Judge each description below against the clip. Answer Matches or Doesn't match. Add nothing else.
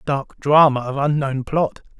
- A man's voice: Matches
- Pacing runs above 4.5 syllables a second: Doesn't match